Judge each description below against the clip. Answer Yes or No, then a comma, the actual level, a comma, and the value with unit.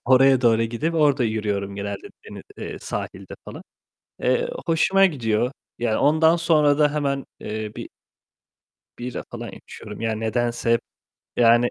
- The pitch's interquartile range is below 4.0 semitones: No, average, 5.0 semitones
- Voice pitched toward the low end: Yes, low, 120 Hz